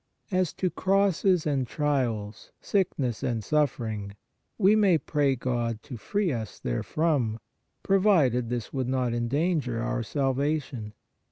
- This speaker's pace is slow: Yes, slow, 120 wpm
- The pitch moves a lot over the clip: Yes, wide, 6.0 semitones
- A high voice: No, low, 135 Hz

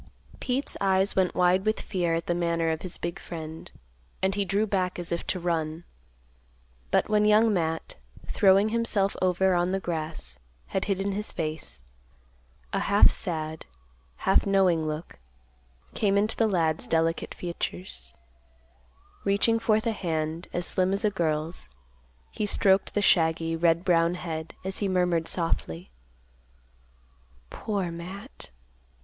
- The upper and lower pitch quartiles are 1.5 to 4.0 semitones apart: Yes, average, 3.2 semitones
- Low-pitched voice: No, medium, 180 Hz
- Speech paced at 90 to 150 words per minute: Yes, average, 145 wpm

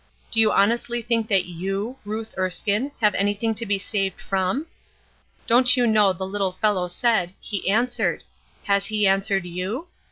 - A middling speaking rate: Yes, average, 160 wpm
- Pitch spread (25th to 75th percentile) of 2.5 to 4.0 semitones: Yes, average, 2.8 semitones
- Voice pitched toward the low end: No, high, 205 Hz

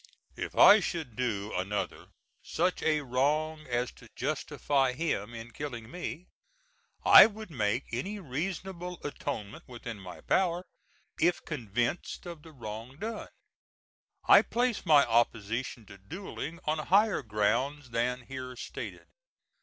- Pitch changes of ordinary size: No, wide, 6.4 semitones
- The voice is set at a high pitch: No, low, 135 Hz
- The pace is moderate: No, slow, 130 wpm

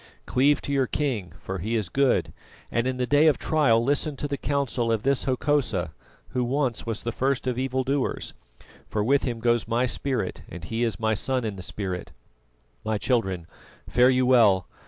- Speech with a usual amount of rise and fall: Yes, average, 3.6 semitones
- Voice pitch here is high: No, low, 125 Hz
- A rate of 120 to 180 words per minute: No, average, 195 wpm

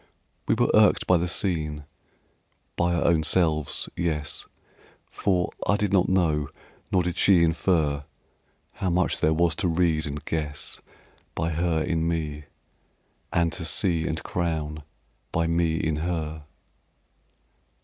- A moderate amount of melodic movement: No, narrow, 2.1 semitones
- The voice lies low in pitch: Yes, very low, 80 Hz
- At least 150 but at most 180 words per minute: No, average, 140 wpm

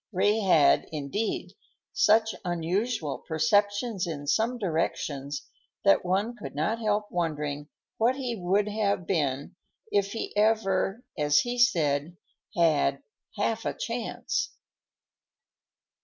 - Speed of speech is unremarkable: No, slow, 115 wpm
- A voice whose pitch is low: No, high, 190 Hz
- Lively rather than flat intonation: Yes, wide, 6.1 semitones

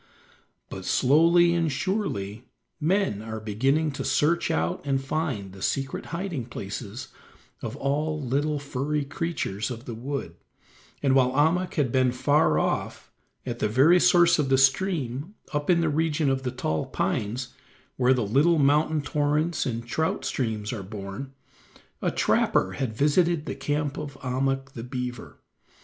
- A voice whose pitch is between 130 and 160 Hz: Yes, low, 135 Hz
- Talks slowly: No, average, 155 wpm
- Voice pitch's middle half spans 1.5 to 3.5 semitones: No, average, 4.3 semitones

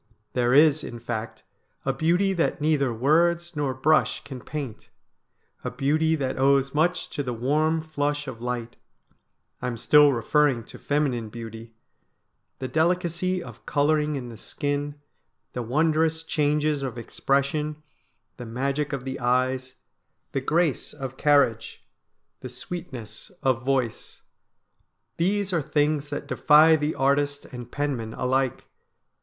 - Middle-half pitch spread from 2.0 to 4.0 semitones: Yes, average, 3.5 semitones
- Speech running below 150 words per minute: Yes, average, 140 wpm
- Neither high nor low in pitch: Yes, medium, 145 Hz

